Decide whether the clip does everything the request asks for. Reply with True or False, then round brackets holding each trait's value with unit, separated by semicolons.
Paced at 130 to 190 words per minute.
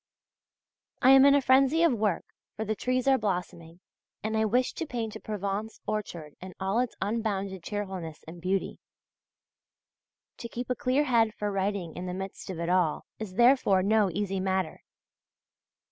True (170 wpm)